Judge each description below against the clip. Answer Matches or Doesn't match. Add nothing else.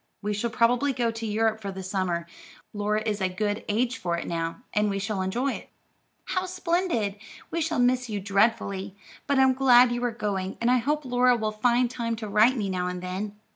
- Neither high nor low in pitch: Doesn't match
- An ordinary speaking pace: Doesn't match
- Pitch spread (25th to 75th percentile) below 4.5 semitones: Matches